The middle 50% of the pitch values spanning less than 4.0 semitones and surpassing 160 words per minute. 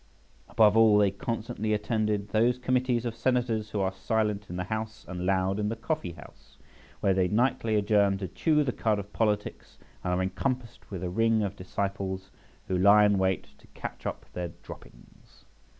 Yes: average, 2.9 semitones; average, 180 wpm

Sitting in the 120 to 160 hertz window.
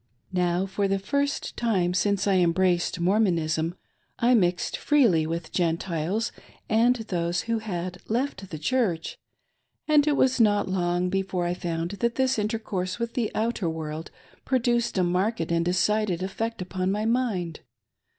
No: high, 190 Hz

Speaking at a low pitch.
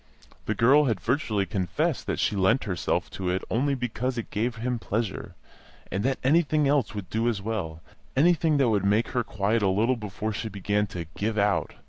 Yes: low, 110 Hz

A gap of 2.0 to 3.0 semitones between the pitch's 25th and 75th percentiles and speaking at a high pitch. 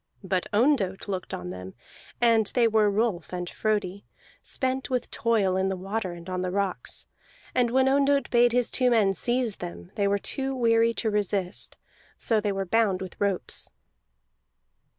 No: average, 4.1 semitones; high, 210 Hz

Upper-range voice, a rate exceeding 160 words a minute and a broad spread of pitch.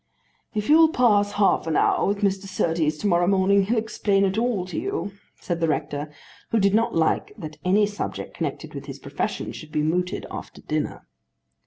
No: high, 195 Hz; average, 190 wpm; average, 4.0 semitones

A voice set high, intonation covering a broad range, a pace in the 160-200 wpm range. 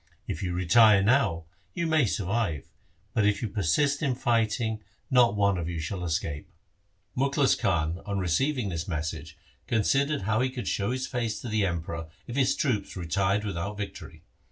No: low, 105 Hz; wide, 5.9 semitones; average, 170 wpm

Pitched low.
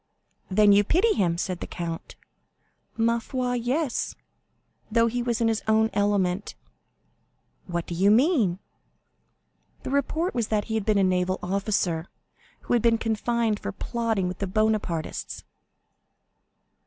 No: high, 215 Hz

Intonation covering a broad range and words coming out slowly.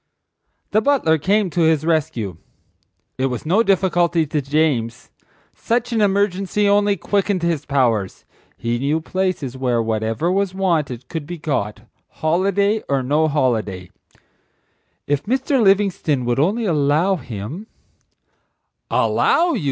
Yes: wide, 6.9 semitones; slow, 130 wpm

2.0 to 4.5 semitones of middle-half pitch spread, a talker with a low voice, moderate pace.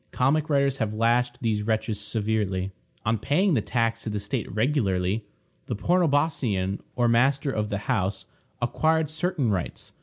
No: average, 5.1 semitones; low, 115 Hz; average, 150 wpm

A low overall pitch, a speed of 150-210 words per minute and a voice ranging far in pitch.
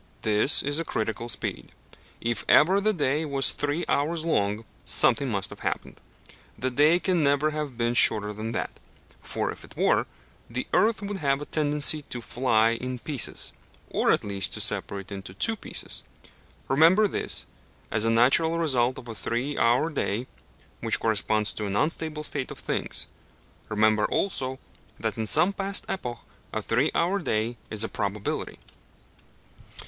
Yes: low, 130 Hz; average, 165 wpm; wide, 6.0 semitones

